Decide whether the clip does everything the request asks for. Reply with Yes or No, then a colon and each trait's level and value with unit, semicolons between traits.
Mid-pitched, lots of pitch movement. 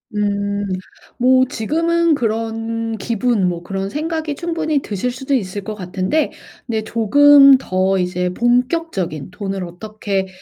No: high, 225 Hz; wide, 6.1 semitones